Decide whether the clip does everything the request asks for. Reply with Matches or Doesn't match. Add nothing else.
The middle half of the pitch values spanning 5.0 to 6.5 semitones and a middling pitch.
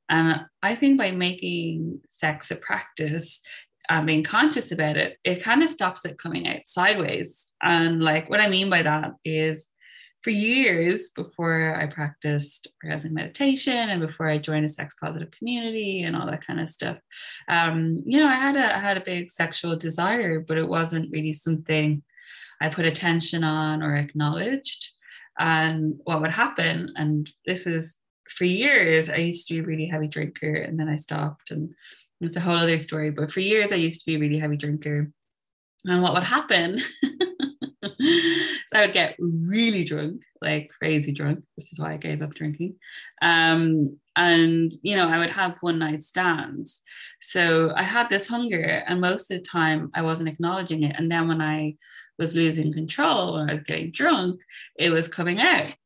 Doesn't match